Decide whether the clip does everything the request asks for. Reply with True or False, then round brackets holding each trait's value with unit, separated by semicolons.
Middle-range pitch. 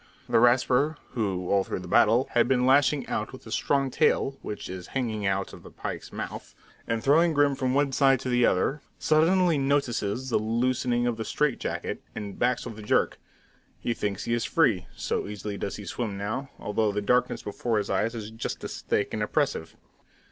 False (120 Hz)